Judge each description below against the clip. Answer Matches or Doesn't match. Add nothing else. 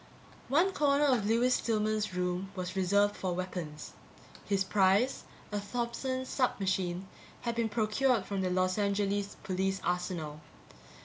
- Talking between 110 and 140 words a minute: Matches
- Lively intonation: Doesn't match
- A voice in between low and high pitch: Doesn't match